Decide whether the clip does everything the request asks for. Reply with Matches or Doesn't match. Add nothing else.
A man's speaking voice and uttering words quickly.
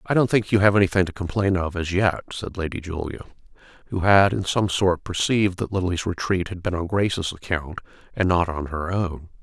Matches